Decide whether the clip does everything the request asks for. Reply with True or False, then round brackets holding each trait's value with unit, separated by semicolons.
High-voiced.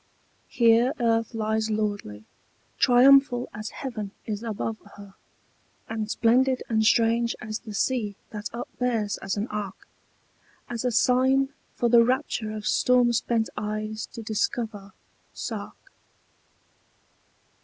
True (225 Hz)